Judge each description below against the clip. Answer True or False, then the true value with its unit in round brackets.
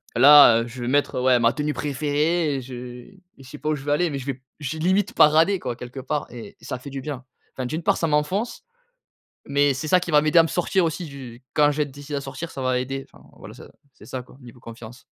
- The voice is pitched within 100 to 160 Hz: True (140 Hz)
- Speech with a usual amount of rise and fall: True (3.2 semitones)